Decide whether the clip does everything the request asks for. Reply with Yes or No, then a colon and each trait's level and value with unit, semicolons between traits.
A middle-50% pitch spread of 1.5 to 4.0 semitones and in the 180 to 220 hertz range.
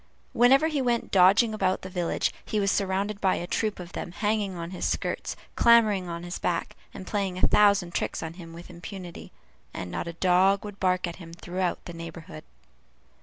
Yes: average, 2.9 semitones; medium, 185 Hz